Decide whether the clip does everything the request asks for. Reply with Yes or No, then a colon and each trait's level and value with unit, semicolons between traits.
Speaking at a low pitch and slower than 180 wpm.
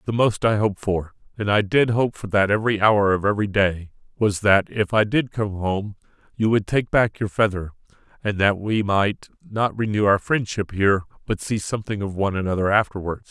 No: low, 105 Hz; average, 190 wpm